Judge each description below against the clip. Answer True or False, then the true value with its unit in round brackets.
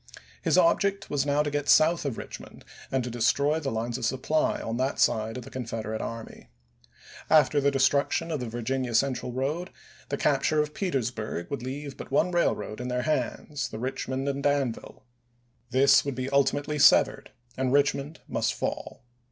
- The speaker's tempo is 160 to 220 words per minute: True (175 wpm)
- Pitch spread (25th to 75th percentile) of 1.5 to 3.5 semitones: True (2.8 semitones)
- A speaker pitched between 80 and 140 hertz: True (135 Hz)